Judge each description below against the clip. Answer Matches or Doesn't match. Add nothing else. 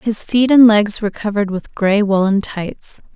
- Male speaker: Doesn't match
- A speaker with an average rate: Matches